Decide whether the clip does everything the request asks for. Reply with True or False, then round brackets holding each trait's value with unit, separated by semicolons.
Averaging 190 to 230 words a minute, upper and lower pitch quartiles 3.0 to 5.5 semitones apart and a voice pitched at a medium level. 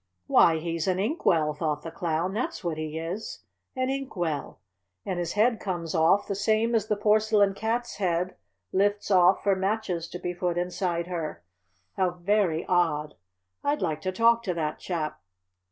False (175 wpm; 3.9 semitones; 180 Hz)